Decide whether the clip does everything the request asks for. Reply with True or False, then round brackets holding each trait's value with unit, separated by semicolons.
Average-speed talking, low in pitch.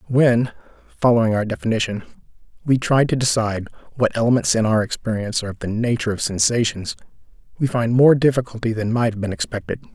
True (170 wpm; 115 Hz)